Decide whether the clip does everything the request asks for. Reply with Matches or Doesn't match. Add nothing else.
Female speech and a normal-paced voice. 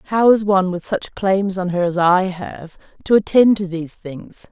Doesn't match